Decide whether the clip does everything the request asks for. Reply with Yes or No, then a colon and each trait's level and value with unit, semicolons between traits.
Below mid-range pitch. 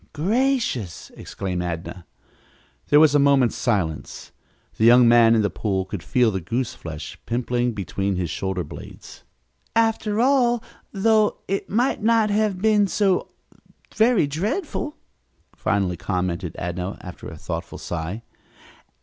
Yes: low, 120 Hz